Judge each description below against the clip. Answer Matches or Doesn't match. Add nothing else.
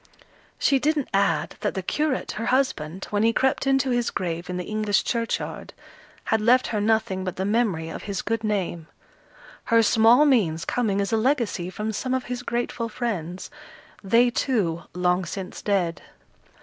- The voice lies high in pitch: Matches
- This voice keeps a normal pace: Matches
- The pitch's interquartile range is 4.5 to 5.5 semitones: Matches